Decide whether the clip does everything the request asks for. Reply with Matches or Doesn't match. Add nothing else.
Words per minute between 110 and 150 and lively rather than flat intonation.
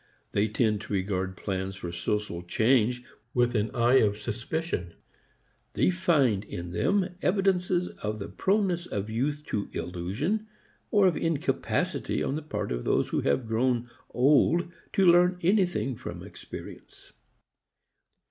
Matches